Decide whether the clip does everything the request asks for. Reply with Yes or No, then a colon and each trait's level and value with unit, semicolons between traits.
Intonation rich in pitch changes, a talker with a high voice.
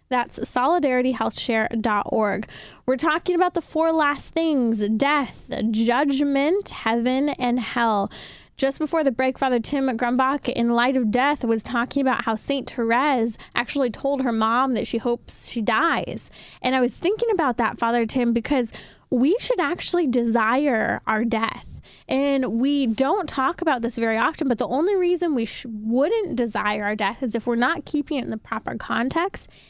No: average, 3.6 semitones; very high, 255 Hz